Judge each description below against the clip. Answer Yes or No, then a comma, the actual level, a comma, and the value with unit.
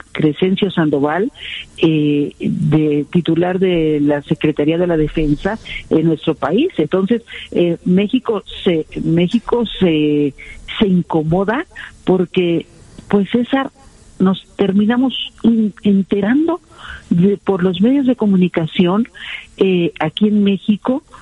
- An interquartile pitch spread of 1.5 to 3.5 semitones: No, average, 4.7 semitones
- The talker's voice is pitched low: No, medium, 185 Hz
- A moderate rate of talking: No, slow, 110 wpm